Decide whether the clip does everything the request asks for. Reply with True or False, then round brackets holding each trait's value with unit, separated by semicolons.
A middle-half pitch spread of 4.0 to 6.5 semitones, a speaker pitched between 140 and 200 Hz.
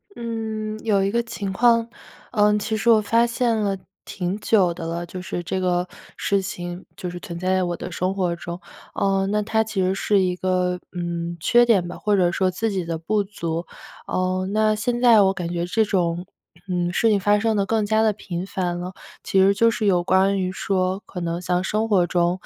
False (3.2 semitones; 190 Hz)